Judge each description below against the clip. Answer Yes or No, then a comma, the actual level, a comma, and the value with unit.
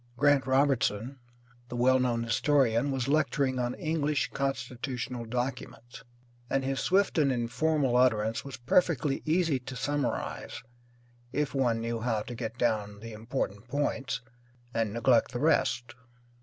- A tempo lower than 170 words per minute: Yes, slow, 135 wpm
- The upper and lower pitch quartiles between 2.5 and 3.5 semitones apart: Yes, average, 3.2 semitones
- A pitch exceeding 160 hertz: No, low, 125 Hz